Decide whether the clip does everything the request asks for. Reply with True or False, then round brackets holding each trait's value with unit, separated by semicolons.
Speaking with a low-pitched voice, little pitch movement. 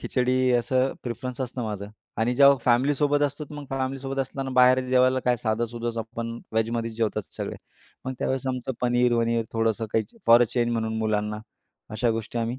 True (120 Hz; 2.3 semitones)